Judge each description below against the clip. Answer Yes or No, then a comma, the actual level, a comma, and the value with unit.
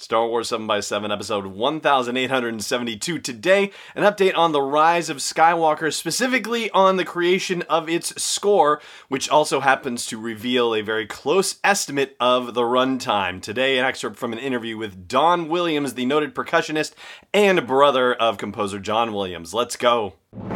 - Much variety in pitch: Yes, wide, 6.5 semitones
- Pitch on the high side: No, medium, 140 Hz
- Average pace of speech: Yes, average, 150 wpm